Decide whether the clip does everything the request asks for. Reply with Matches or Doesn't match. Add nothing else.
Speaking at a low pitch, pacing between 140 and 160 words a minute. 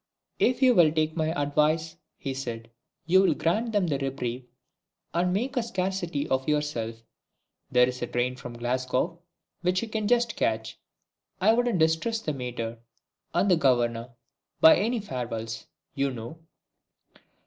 Doesn't match